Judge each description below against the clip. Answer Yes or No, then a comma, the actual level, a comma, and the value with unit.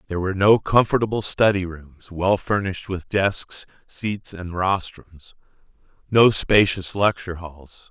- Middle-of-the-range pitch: No, very low, 95 Hz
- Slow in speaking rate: Yes, slow, 130 wpm